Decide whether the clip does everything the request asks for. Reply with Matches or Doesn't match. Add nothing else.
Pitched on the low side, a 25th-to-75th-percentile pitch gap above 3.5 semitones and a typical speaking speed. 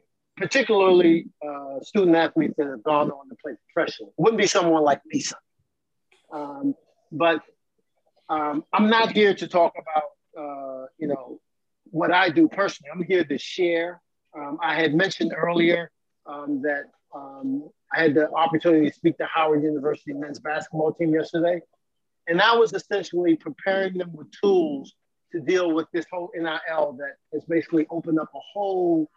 Doesn't match